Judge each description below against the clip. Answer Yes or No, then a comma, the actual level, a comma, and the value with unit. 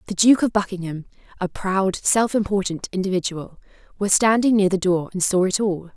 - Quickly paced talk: No, average, 180 wpm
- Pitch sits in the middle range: No, high, 195 Hz